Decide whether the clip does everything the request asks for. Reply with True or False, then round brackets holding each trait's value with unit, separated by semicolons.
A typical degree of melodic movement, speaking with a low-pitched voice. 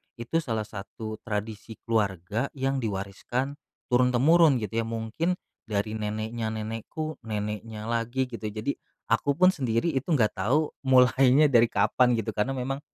True (3.7 semitones; 115 Hz)